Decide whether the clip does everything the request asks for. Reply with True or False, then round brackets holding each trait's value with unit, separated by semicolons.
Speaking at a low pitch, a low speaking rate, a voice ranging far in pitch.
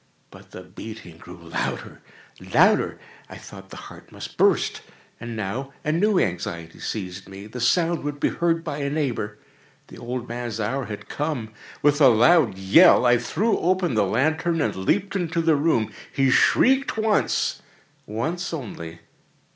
False (130 Hz; 155 wpm; 7.7 semitones)